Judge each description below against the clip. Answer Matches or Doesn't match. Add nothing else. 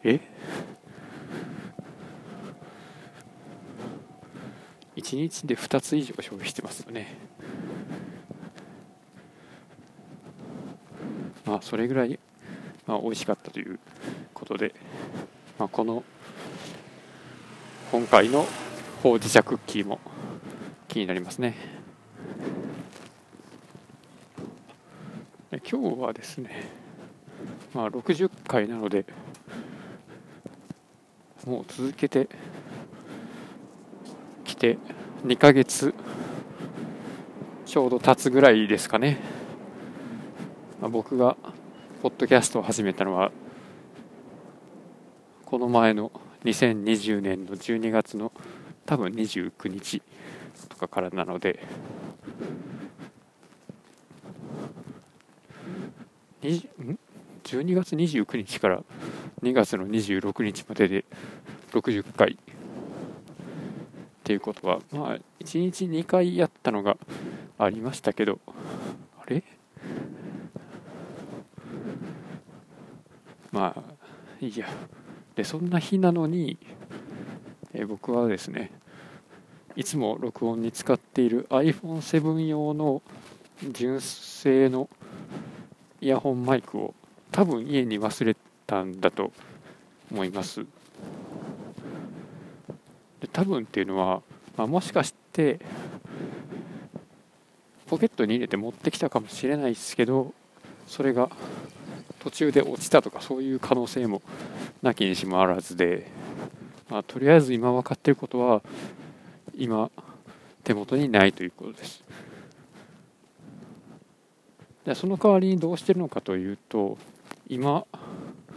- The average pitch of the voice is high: Doesn't match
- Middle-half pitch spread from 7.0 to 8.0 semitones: Doesn't match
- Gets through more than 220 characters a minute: Doesn't match